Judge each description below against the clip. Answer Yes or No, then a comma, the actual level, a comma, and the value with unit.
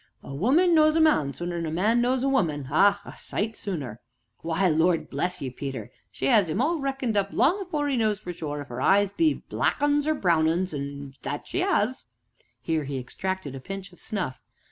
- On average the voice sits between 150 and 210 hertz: Yes, high, 190 Hz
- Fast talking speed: Yes, fast, 210 wpm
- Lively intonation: Yes, wide, 9.0 semitones